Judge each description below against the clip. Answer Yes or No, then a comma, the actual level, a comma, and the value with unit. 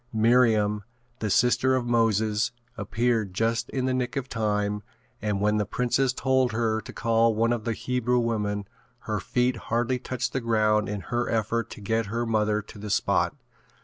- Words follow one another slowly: No, average, 180 wpm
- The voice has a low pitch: Yes, low, 115 Hz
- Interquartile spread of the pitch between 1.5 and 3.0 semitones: Yes, narrow, 2.4 semitones